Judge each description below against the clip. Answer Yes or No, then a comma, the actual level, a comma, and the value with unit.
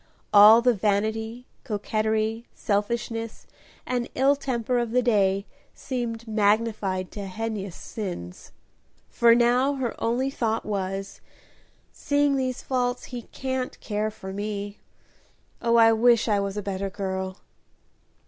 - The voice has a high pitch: Yes, high, 220 Hz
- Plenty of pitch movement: No, average, 3.0 semitones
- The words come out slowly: Yes, slow, 125 wpm